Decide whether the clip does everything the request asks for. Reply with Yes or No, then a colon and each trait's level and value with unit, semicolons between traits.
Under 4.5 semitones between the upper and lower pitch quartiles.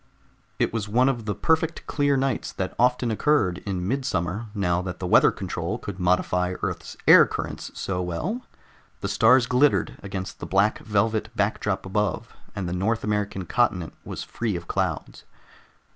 No: average, 4.9 semitones